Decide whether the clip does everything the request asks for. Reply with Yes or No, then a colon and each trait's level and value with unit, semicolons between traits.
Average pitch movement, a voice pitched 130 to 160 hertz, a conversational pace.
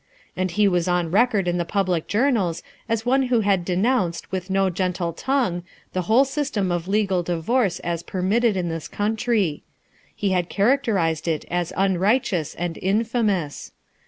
No: average, 4.1 semitones; high, 190 Hz; average, 160 wpm